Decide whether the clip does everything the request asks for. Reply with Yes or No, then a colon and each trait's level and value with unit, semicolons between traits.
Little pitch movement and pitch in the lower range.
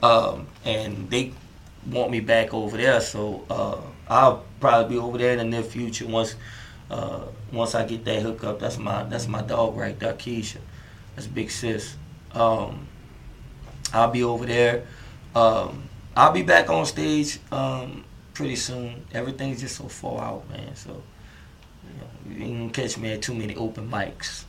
Yes: narrow, 1.8 semitones; low, 115 Hz